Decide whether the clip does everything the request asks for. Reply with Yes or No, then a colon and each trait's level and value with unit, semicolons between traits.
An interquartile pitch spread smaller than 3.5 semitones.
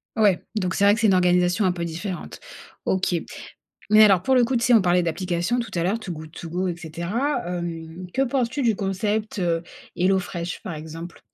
No: average, 3.9 semitones